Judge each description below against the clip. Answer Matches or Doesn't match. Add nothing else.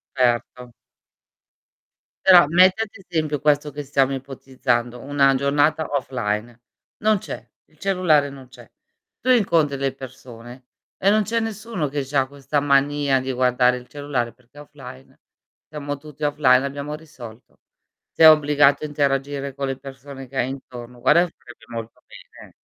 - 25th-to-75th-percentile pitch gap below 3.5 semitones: Matches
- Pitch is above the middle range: Doesn't match